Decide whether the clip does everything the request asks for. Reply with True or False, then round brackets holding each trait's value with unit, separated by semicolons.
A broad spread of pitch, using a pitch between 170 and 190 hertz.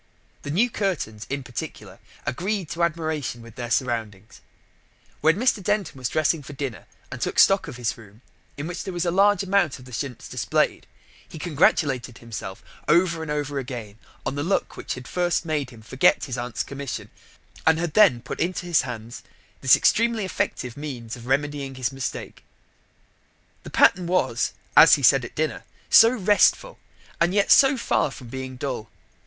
False (6.2 semitones; 145 Hz)